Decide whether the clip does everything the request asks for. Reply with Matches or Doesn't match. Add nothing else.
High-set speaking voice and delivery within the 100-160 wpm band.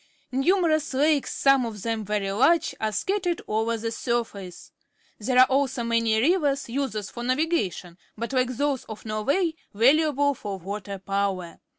Matches